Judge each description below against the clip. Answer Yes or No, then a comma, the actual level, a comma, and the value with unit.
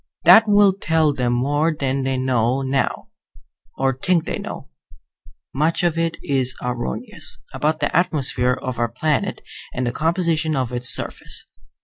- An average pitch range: Yes, average, 4.1 semitones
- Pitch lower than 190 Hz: Yes, low, 135 Hz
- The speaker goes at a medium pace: Yes, average, 150 wpm